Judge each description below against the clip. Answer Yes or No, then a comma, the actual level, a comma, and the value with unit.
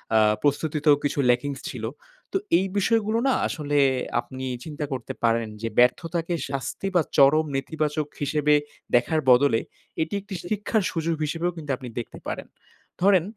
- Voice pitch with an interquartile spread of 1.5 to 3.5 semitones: No, average, 3.9 semitones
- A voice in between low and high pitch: Yes, medium, 150 Hz